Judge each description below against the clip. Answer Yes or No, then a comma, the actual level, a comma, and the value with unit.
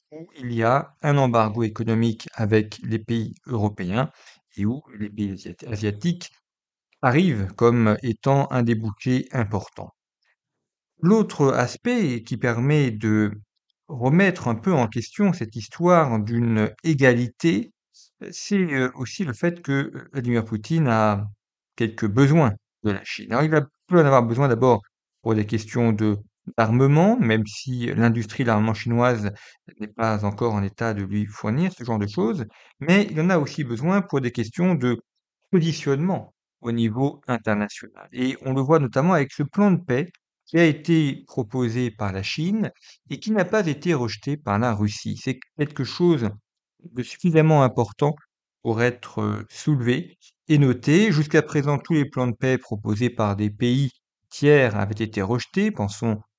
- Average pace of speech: Yes, average, 155 wpm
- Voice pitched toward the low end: Yes, low, 125 Hz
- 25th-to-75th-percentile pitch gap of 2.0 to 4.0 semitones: No, wide, 5.5 semitones